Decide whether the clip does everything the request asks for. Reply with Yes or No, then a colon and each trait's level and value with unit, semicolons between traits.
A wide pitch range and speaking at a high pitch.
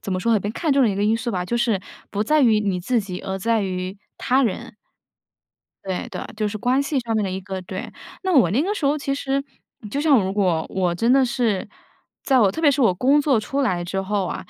Yes: wide, 5.9 semitones; high, 220 Hz